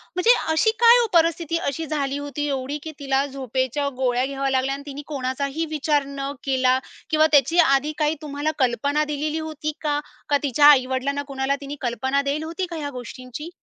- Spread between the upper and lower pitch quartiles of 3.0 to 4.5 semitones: No, narrow, 2.4 semitones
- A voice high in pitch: Yes, very high, 280 Hz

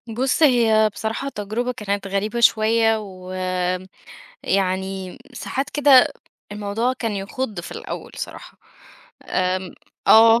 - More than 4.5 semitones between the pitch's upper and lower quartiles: No, average, 3.5 semitones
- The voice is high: Yes, high, 220 Hz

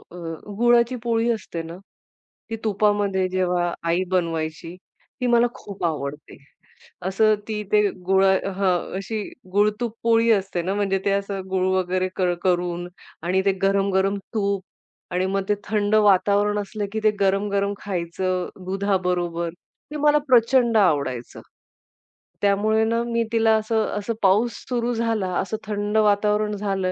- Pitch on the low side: No, high, 200 Hz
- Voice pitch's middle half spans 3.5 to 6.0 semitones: No, average, 2.8 semitones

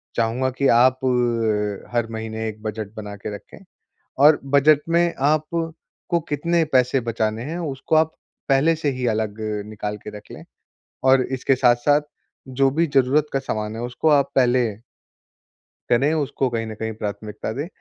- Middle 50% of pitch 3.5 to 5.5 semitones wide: Yes, average, 4.4 semitones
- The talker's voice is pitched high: No, low, 125 Hz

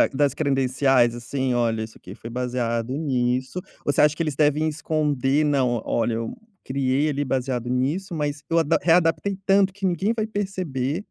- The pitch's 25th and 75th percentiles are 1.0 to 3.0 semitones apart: No, average, 4.2 semitones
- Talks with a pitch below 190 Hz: Yes, medium, 140 Hz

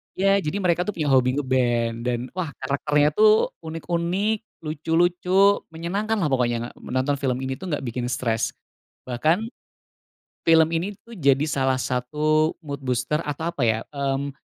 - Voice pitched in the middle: Yes, medium, 150 Hz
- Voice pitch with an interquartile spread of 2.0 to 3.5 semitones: No, average, 4.6 semitones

